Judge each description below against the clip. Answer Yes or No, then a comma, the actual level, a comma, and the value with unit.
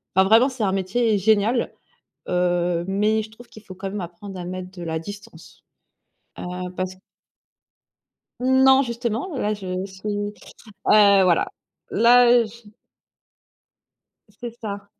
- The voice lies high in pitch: Yes, high, 205 Hz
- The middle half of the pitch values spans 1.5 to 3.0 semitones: No, average, 4.0 semitones